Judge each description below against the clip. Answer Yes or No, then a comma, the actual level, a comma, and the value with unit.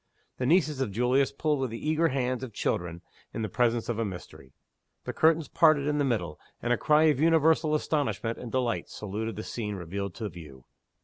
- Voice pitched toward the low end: Yes, low, 125 Hz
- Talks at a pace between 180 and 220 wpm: Yes, average, 200 wpm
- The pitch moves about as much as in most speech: No, wide, 6.1 semitones